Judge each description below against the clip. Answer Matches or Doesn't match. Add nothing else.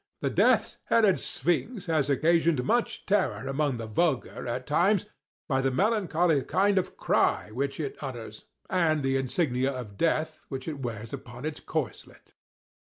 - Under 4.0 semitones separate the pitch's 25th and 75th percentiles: Doesn't match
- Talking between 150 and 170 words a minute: Matches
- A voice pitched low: Doesn't match